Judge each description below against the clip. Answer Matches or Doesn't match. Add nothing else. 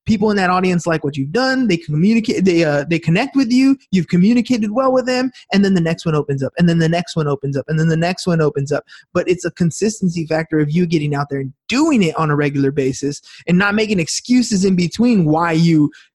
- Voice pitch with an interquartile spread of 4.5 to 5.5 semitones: Matches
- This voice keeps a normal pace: Doesn't match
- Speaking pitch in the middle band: Matches